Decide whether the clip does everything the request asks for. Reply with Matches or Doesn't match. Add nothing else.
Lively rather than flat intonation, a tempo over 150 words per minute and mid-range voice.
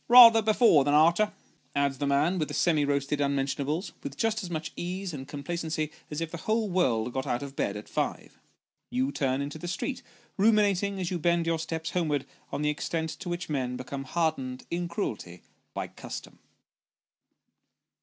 Doesn't match